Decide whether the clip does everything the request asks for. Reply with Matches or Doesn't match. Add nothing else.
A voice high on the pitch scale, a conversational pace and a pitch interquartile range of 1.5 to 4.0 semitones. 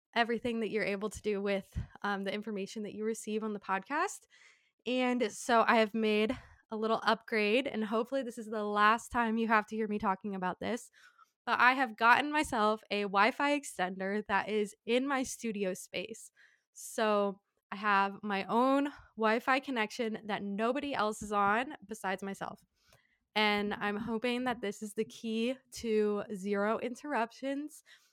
Matches